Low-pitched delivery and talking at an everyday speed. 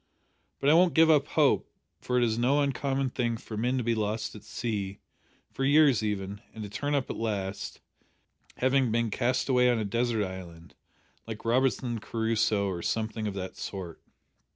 Yes: low, 115 Hz; average, 180 wpm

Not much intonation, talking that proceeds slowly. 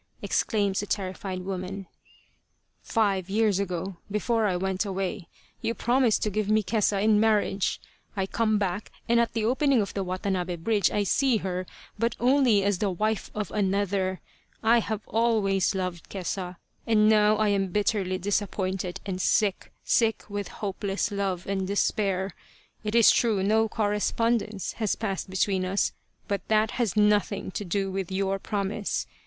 No: narrow, 2.2 semitones; average, 160 wpm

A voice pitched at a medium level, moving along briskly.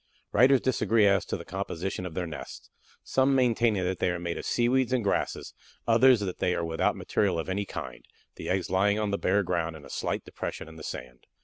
No: very low, 95 Hz; fast, 220 wpm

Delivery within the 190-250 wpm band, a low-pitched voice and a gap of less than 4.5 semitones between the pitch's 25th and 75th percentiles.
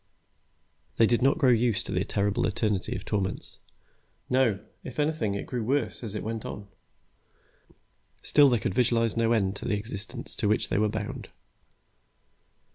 No: average, 165 wpm; low, 110 Hz; average, 3.0 semitones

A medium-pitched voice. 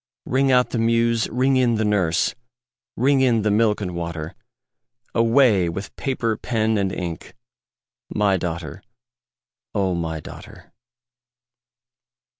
No: low, 105 Hz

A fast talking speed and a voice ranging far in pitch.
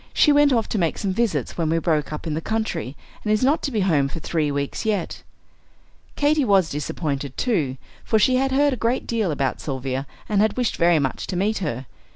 Yes: fast, 220 wpm; wide, 7.5 semitones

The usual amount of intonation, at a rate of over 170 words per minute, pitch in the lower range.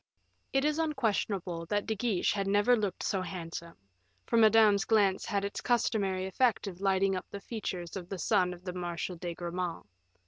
No: average, 3.3 semitones; average, 180 wpm; high, 195 Hz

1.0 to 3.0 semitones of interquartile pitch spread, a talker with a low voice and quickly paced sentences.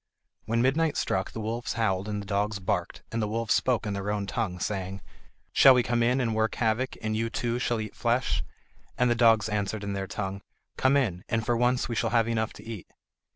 Yes: average, 2.7 semitones; low, 110 Hz; fast, 225 wpm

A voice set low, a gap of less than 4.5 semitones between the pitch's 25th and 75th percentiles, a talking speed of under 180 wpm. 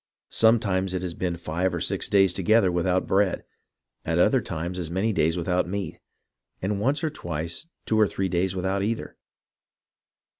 Yes: very low, 95 Hz; narrow, 2.5 semitones; average, 165 wpm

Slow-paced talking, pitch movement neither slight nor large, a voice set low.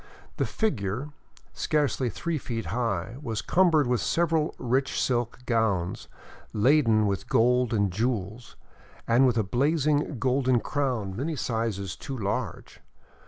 Yes: slow, 125 wpm; average, 4.4 semitones; low, 120 Hz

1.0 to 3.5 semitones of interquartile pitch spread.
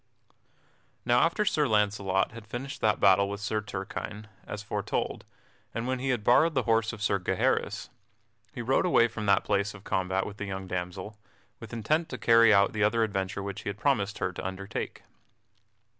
Yes: average, 2.9 semitones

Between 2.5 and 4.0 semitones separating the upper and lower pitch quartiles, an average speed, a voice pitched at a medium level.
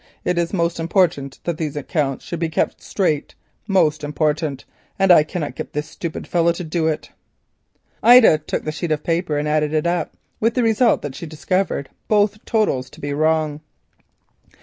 Yes: average, 3.0 semitones; average, 180 wpm; medium, 160 Hz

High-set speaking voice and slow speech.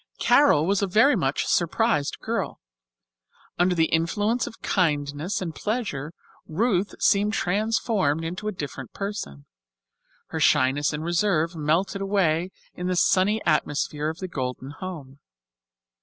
No: medium, 175 Hz; slow, 130 wpm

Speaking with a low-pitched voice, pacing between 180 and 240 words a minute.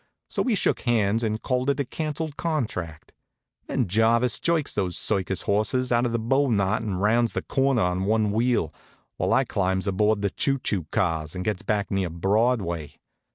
Yes: low, 110 Hz; average, 185 wpm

